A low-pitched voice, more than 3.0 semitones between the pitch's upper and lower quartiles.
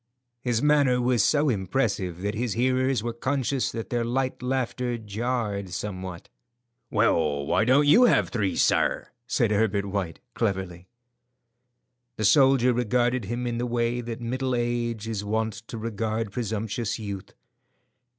Yes: low, 115 Hz; average, 3.4 semitones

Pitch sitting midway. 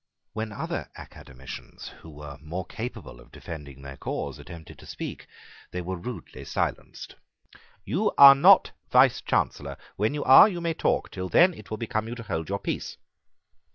No: low, 100 Hz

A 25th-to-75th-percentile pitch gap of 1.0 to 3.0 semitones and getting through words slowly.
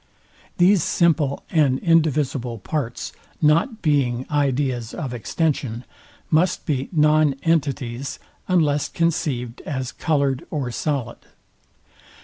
No: average, 3.5 semitones; slow, 100 wpm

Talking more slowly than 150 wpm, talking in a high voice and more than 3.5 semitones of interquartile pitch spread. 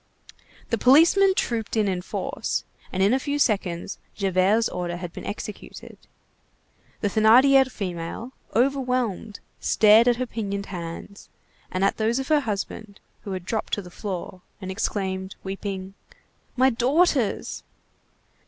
Yes: slow, 135 wpm; high, 210 Hz; average, 4.8 semitones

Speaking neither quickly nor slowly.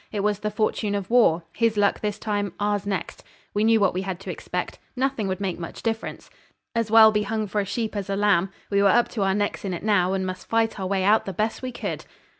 No: fast, 260 wpm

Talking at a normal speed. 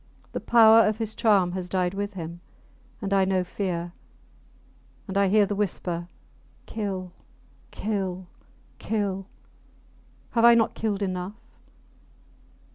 No: slow, 120 wpm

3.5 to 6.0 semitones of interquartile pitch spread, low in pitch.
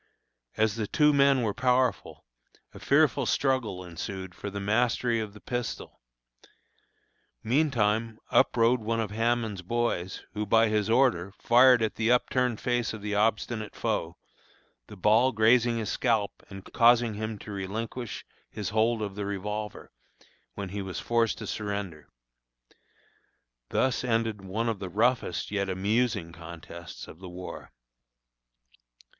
No: average, 2.9 semitones; low, 110 Hz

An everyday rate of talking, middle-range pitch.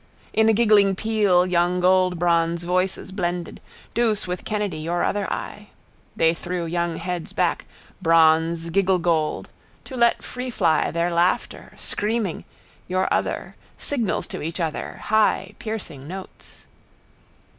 No: slow, 125 wpm; medium, 180 Hz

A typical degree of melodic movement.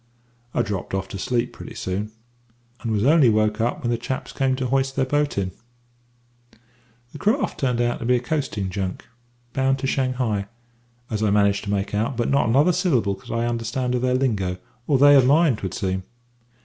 Yes: average, 4.4 semitones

